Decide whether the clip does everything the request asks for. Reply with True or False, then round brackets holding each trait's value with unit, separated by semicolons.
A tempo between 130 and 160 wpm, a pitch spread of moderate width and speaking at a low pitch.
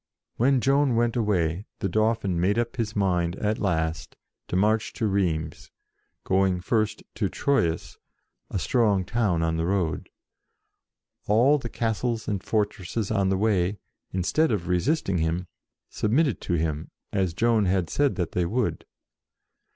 True (145 wpm; 4.4 semitones; 100 Hz)